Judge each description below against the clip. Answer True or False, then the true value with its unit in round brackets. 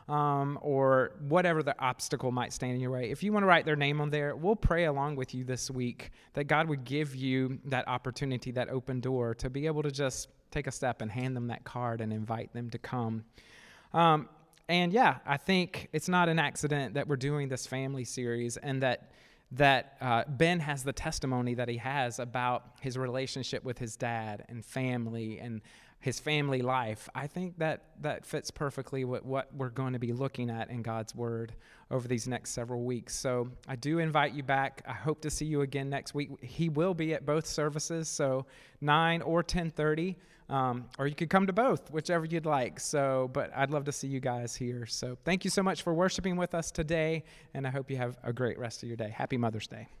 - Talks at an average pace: False (220 wpm)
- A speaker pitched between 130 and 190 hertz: True (135 Hz)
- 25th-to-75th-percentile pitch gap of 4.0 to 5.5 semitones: False (3.5 semitones)